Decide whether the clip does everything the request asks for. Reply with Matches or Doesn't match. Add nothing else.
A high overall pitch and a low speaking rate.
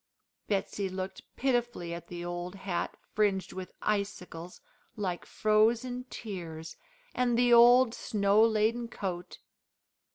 Matches